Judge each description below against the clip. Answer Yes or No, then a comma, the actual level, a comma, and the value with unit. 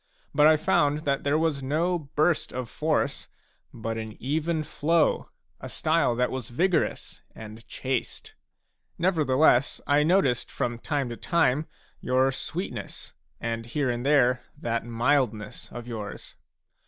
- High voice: No, low, 135 Hz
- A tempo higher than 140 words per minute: No, slow, 135 wpm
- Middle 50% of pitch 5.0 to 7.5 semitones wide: No, average, 4.5 semitones